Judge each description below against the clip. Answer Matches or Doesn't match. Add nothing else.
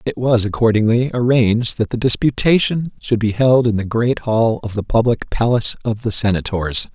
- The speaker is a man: Matches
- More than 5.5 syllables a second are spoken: Doesn't match